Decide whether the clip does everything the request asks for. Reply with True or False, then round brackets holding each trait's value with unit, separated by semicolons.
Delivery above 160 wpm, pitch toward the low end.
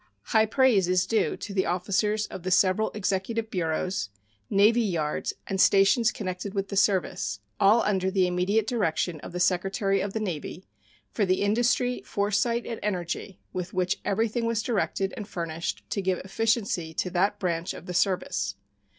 False (170 wpm; 195 Hz)